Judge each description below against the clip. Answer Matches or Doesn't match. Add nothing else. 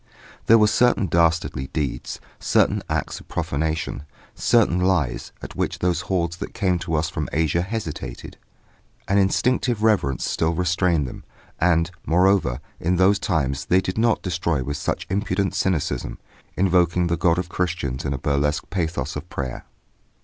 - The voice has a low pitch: Matches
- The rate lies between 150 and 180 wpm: Matches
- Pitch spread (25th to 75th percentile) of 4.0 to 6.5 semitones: Doesn't match